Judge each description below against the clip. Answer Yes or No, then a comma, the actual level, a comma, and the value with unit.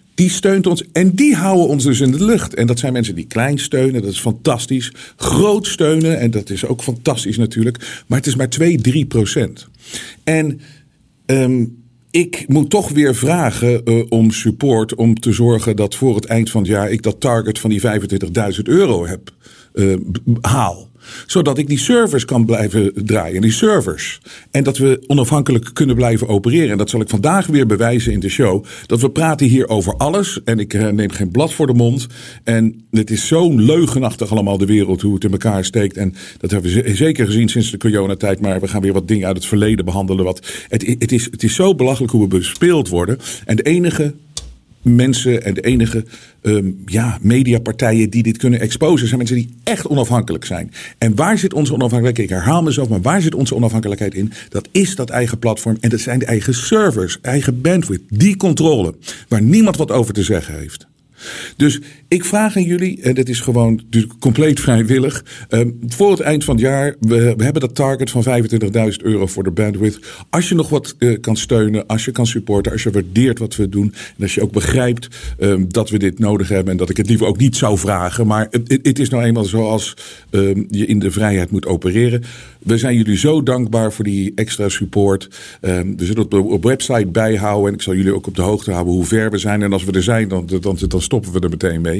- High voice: No, low, 115 Hz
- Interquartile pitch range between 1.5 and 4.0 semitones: No, average, 4.5 semitones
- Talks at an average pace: No, fast, 205 wpm